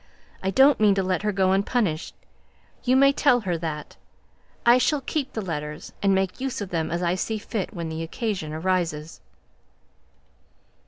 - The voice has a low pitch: No, high, 190 Hz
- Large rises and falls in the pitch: Yes, wide, 5.8 semitones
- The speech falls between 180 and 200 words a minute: No, average, 170 wpm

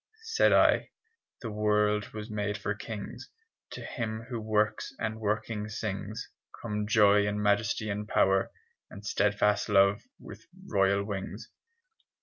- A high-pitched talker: No, low, 105 Hz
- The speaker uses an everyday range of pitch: No, narrow, 1.1 semitones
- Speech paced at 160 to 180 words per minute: No, slow, 135 wpm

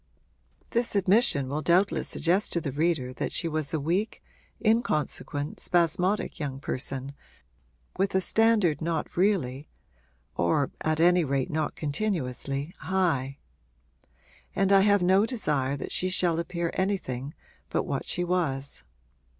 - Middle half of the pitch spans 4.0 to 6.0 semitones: Yes, average, 5.1 semitones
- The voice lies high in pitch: No, medium, 165 Hz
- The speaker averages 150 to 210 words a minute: No, slow, 135 wpm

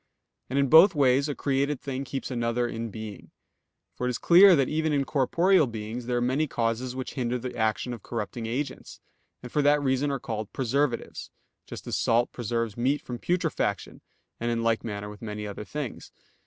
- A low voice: Yes, low, 125 Hz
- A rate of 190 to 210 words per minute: Yes, average, 195 wpm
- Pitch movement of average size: Yes, average, 3.5 semitones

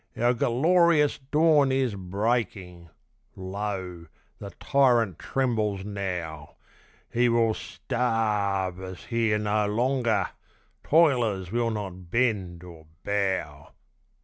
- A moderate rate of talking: No, slow, 105 wpm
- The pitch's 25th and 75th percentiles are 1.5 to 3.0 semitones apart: No, average, 4.5 semitones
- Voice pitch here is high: No, low, 105 Hz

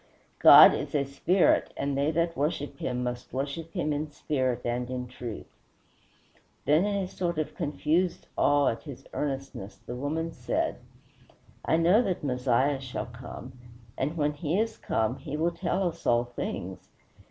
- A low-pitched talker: No, medium, 145 Hz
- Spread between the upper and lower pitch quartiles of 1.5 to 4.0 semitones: No, average, 4.7 semitones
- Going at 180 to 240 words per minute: No, average, 165 wpm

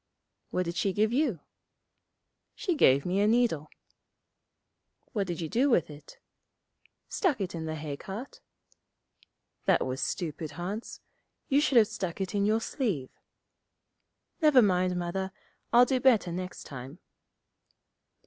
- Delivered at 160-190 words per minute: No, average, 140 wpm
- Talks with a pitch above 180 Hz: Yes, high, 190 Hz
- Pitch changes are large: Yes, wide, 5.9 semitones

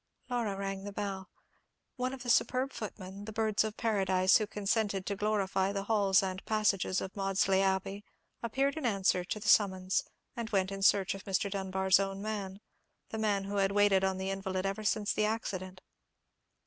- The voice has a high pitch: Yes, high, 195 Hz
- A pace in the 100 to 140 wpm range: No, average, 180 wpm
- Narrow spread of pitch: Yes, narrow, 1.9 semitones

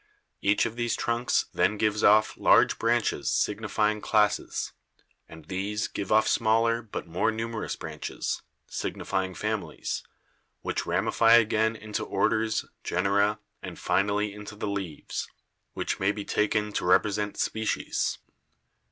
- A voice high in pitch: No, low, 105 Hz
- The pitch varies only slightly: Yes, narrow, 1.6 semitones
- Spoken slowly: Yes, slow, 125 wpm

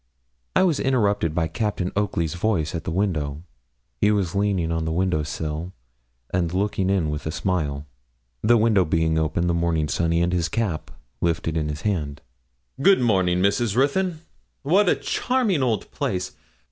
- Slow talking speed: No, average, 165 wpm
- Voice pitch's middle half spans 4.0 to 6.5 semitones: Yes, average, 4.6 semitones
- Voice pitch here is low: Yes, very low, 90 Hz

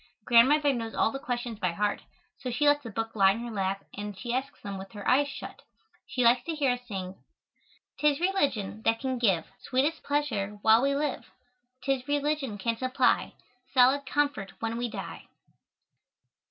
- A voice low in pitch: No, high, 245 Hz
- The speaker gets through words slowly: No, average, 180 wpm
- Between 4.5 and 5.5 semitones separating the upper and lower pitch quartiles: Yes, average, 5.1 semitones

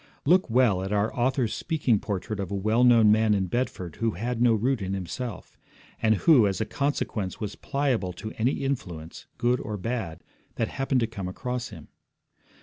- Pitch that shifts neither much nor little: Yes, average, 4.2 semitones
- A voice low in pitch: Yes, low, 110 Hz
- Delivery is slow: No, average, 185 wpm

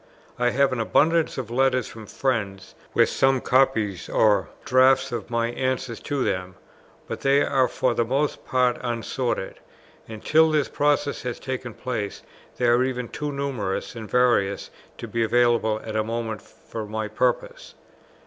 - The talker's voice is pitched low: Yes, low, 125 Hz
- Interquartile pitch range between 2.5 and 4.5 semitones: Yes, average, 3.1 semitones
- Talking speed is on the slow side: No, average, 160 wpm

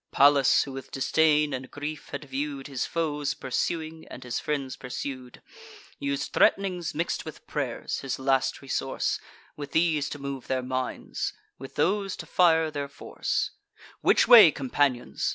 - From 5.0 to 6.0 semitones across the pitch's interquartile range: No, average, 2.9 semitones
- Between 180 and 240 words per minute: No, average, 150 wpm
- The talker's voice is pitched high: No, medium, 140 Hz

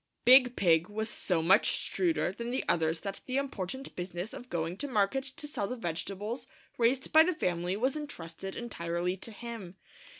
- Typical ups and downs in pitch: No, wide, 6.4 semitones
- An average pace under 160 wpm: No, average, 175 wpm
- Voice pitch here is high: Yes, high, 210 Hz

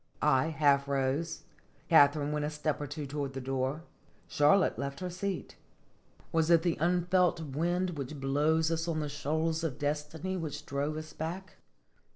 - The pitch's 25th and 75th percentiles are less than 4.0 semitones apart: Yes, narrow, 2.5 semitones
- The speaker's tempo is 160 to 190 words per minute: Yes, average, 165 wpm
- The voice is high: No, medium, 155 Hz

